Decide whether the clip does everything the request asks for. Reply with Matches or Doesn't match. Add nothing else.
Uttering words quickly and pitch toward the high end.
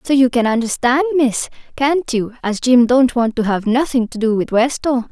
Matches